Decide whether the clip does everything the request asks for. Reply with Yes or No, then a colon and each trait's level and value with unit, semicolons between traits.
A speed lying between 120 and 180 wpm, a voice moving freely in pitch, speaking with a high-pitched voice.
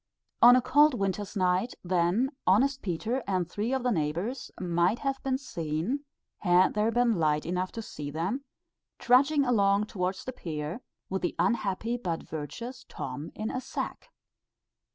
Yes: average, 155 wpm; wide, 5.9 semitones; high, 205 Hz